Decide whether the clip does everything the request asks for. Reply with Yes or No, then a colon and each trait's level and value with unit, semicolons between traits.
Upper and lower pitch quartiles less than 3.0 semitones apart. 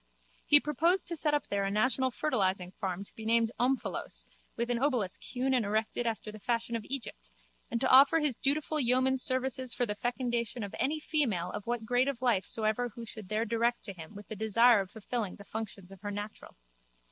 No: average, 3.8 semitones